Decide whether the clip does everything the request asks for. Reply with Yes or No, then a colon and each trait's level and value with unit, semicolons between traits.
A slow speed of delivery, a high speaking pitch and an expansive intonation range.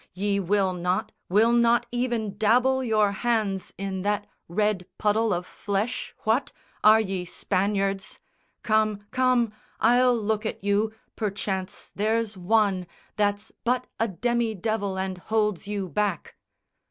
No: slow, 130 wpm; high, 210 Hz; narrow, 2.6 semitones